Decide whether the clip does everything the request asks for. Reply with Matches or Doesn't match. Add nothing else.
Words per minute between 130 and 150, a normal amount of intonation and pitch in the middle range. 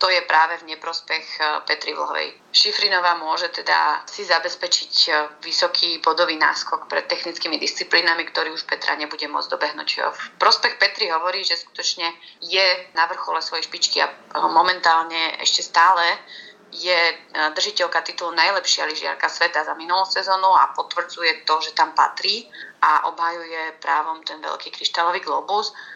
Doesn't match